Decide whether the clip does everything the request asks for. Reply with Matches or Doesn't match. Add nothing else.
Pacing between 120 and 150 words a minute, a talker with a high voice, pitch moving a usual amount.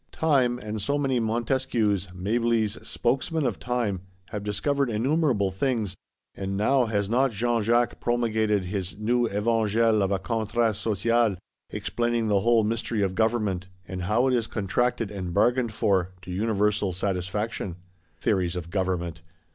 Doesn't match